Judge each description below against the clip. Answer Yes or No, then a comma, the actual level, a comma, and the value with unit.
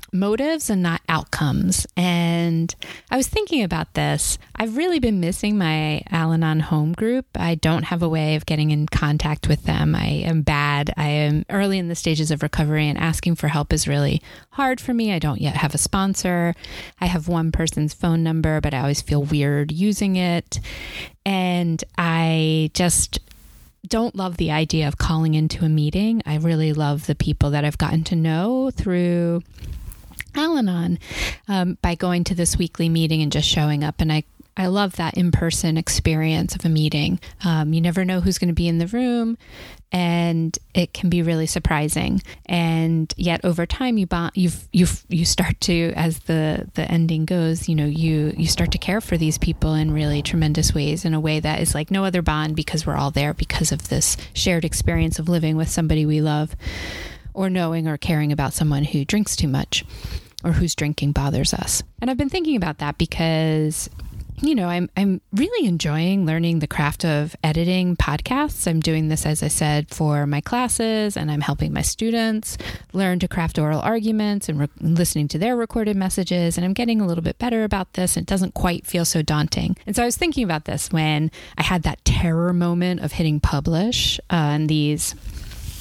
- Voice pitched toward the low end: No, medium, 165 Hz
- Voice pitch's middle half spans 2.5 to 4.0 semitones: Yes, average, 3.2 semitones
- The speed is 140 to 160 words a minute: No, average, 195 wpm